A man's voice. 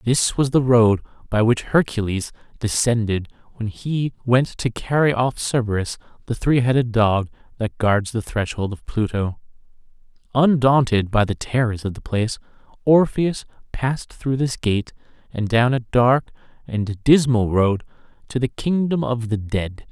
Yes: male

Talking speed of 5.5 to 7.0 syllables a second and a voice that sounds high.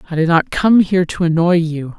No: 5.6 syllables/s; medium, 170 Hz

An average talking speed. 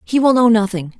No: fast, 240 wpm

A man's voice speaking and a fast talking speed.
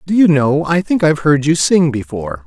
Yes: male; fast, 245 wpm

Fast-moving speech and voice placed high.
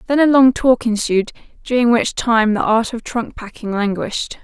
No: average, 190 wpm; high, 230 Hz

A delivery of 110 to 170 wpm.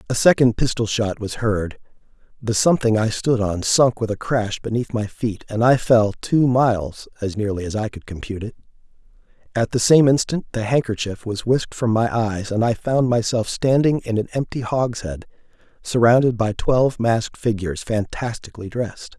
No: average, 180 wpm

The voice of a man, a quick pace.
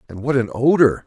Yes: male; fast, 225 wpm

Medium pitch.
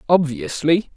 Yes: medium, 170 Hz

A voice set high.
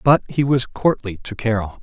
No: low, 120 Hz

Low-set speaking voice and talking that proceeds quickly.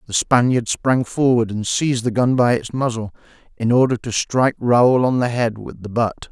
Yes: low, 120 Hz; fast, 210 wpm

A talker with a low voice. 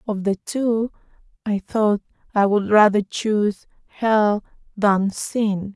No: high, 210 Hz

